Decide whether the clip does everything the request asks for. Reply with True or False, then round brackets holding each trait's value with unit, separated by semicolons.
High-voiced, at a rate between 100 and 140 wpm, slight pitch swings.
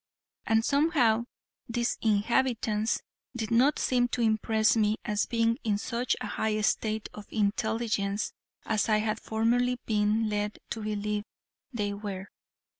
True (220 Hz; 135 wpm; 1.9 semitones)